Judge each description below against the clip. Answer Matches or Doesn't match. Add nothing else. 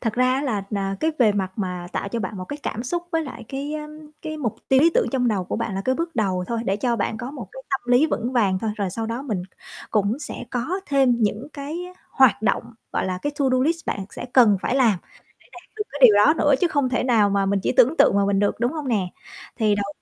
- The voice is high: Matches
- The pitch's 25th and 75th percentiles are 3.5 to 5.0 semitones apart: Doesn't match